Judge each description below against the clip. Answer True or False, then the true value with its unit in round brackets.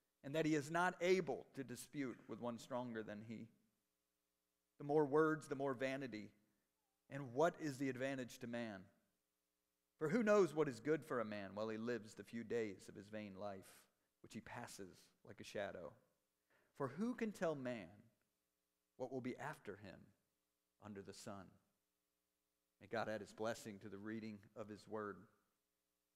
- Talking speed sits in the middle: True (170 wpm)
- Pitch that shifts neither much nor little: False (6.1 semitones)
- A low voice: True (110 Hz)